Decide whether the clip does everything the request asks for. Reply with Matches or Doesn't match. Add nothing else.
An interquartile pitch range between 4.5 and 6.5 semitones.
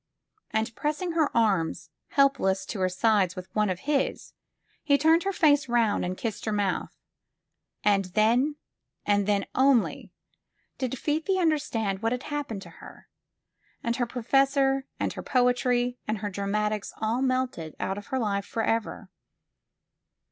Matches